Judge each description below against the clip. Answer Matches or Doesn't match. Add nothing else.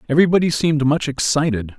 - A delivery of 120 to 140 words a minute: Matches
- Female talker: Doesn't match